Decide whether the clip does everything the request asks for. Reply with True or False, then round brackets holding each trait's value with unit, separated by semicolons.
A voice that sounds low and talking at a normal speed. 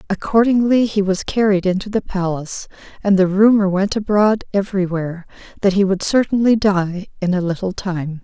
False (195 Hz; 170 wpm)